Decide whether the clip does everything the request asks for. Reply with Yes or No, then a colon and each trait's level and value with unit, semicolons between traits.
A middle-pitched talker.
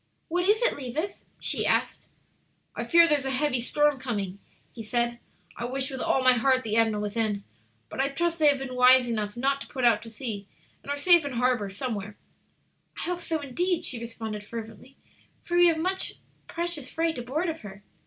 No: very high, 260 Hz